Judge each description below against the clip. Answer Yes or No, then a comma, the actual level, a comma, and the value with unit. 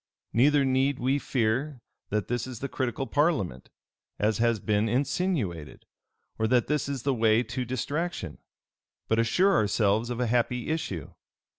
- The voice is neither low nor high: No, low, 125 Hz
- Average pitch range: Yes, average, 4.1 semitones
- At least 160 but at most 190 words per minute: No, average, 150 wpm